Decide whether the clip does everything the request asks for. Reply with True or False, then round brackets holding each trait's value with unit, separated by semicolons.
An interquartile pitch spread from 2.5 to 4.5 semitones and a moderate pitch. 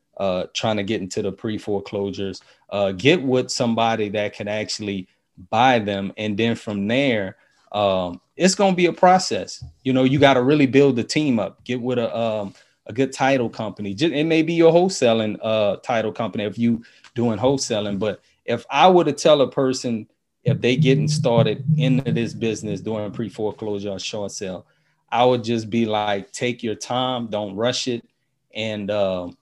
False (4.1 semitones; 115 Hz)